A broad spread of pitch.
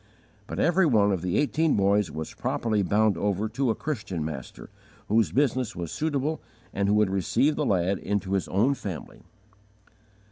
Yes: wide, 5.8 semitones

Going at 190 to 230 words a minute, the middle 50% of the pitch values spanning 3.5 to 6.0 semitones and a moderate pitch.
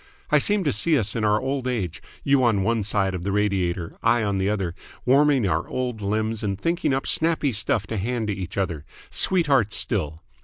No: fast, 205 wpm; average, 5.0 semitones; low, 110 Hz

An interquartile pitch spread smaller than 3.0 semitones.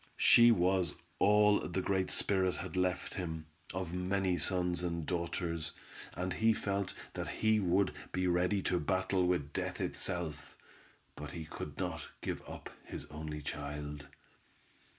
Yes: narrow, 2.4 semitones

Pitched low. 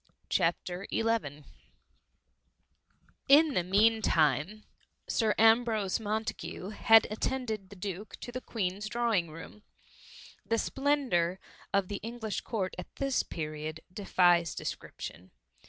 No: high, 210 Hz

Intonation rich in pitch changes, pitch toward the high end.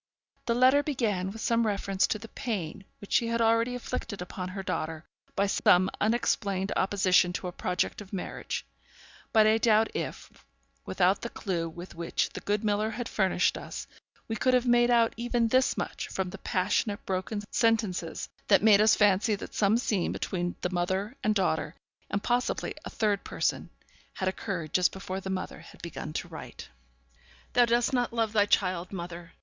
No: average, 3.6 semitones; high, 205 Hz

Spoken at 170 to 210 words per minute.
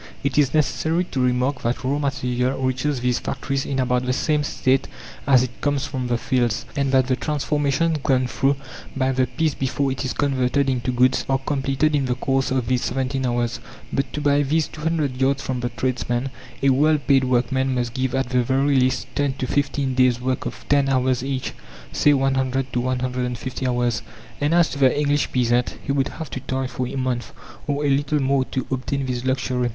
Yes: fast, 205 wpm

